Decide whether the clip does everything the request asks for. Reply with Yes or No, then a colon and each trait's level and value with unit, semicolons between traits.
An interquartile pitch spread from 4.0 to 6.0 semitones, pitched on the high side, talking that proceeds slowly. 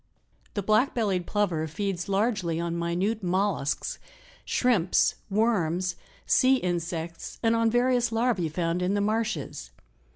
Yes: average, 4.7 semitones; high, 195 Hz; slow, 125 wpm